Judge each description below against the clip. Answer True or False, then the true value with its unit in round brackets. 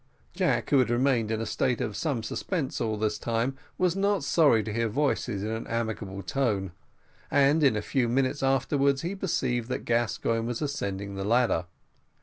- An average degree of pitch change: True (4.0 semitones)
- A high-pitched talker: False (120 Hz)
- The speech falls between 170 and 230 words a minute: True (180 wpm)